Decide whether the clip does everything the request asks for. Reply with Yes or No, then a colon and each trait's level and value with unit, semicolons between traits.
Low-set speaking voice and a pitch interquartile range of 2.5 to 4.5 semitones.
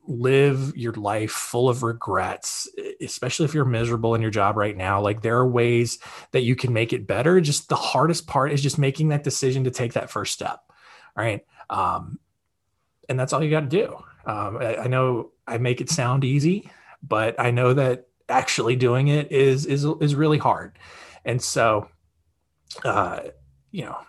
Yes: low, 125 Hz; average, 3.7 semitones